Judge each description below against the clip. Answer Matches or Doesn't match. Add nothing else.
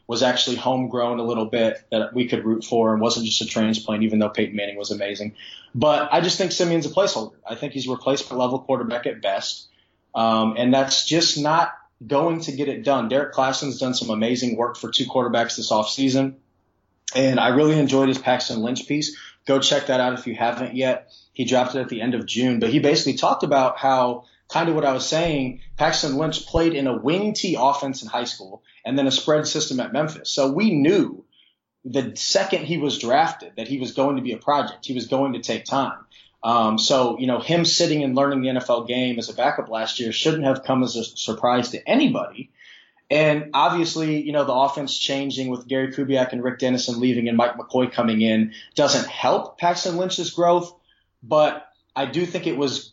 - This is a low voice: Matches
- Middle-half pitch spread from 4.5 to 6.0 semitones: Doesn't match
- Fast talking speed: Matches